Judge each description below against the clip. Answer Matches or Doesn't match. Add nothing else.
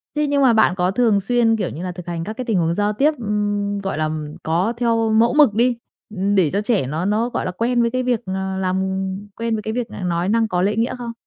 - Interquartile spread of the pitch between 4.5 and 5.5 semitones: Doesn't match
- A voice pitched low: Doesn't match